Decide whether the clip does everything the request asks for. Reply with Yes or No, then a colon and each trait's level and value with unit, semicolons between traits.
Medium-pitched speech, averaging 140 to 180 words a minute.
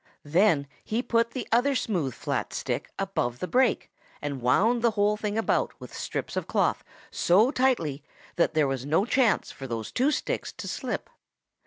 No: high, 205 Hz; average, 170 wpm